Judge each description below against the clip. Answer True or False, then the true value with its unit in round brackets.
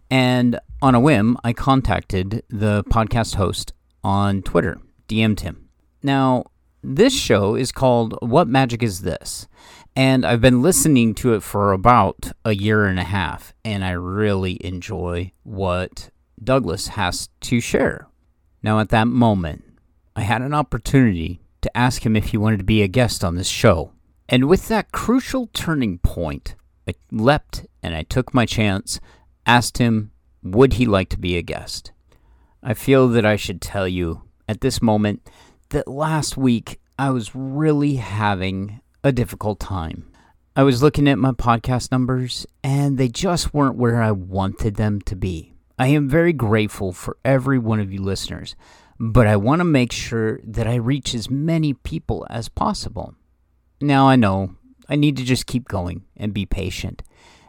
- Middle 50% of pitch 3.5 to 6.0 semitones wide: True (5.5 semitones)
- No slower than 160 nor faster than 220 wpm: True (165 wpm)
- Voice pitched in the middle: False (110 Hz)